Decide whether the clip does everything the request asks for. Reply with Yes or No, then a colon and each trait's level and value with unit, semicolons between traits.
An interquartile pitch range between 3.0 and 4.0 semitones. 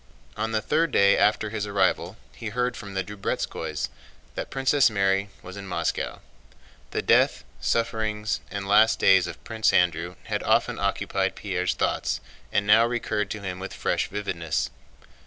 No: narrow, 2.5 semitones